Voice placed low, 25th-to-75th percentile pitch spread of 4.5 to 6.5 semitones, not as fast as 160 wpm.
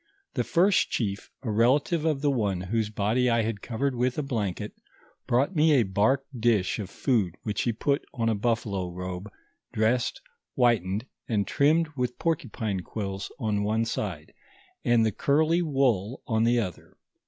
No: low, 115 Hz; average, 4.8 semitones; average, 165 wpm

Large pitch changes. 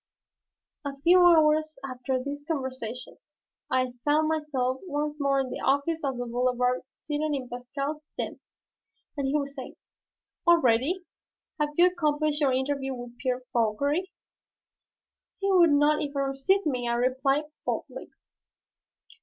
No: average, 3.1 semitones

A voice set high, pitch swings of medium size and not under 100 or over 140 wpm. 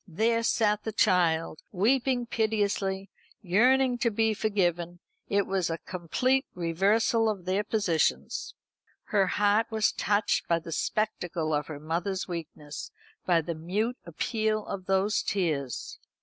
Yes: high, 195 Hz; average, 4.3 semitones; slow, 135 wpm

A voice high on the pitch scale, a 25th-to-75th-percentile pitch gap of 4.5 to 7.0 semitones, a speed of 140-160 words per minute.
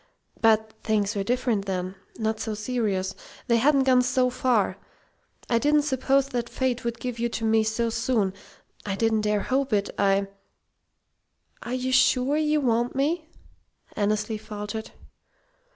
No: high, 230 Hz; average, 3.4 semitones; average, 150 wpm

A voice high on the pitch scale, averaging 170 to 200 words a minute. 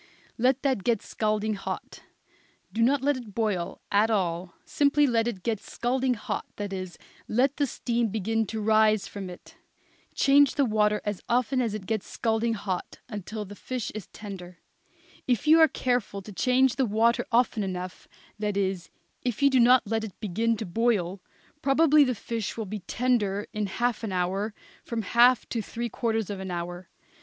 Yes: high, 220 Hz; average, 180 wpm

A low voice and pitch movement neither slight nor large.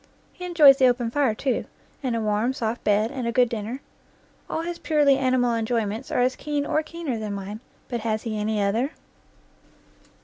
No: high, 245 Hz; average, 3.9 semitones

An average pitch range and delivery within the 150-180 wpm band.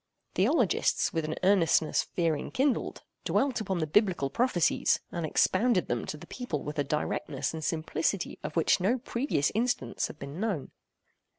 No: wide, 6.2 semitones; average, 160 wpm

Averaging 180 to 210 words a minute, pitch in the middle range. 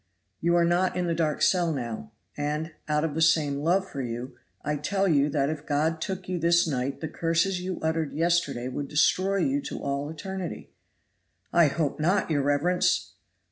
Yes: average, 185 wpm; medium, 160 Hz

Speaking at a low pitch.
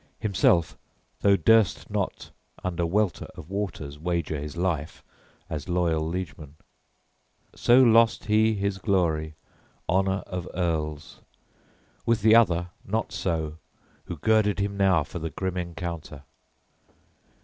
Yes: very low, 90 Hz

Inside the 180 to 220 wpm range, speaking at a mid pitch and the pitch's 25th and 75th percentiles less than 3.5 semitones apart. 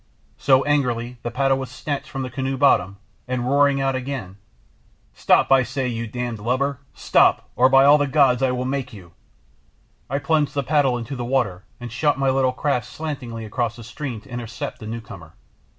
No: average, 190 wpm; low, 130 Hz; narrow, 2.5 semitones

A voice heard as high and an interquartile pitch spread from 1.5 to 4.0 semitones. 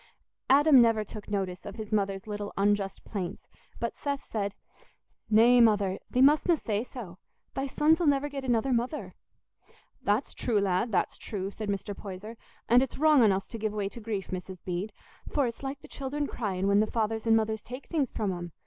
No: high, 220 Hz; average, 4.4 semitones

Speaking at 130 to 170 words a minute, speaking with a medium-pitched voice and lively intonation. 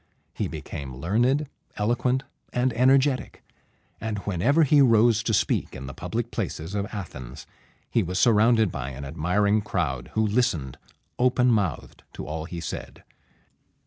No: average, 145 wpm; low, 105 Hz; wide, 7.0 semitones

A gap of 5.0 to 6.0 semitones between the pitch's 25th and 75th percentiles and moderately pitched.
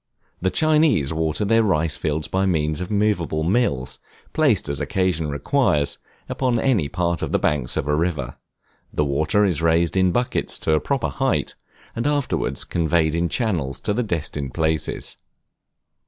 No: wide, 5.5 semitones; very low, 85 Hz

